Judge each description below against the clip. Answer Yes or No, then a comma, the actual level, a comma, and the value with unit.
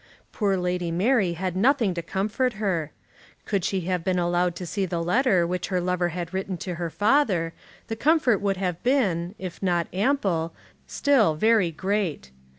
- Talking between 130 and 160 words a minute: No, average, 170 wpm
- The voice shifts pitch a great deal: No, average, 3.5 semitones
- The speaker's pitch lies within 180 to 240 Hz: Yes, medium, 185 Hz